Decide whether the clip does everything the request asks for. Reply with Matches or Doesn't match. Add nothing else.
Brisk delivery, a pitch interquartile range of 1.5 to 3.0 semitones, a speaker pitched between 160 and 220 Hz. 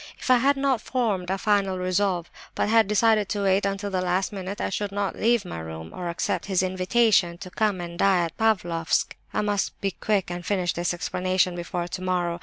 Matches